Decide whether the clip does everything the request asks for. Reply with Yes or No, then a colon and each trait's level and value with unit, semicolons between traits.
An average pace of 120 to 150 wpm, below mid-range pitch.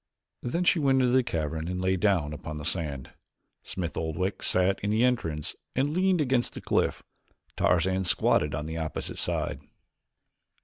No: average, 165 wpm; very low, 95 Hz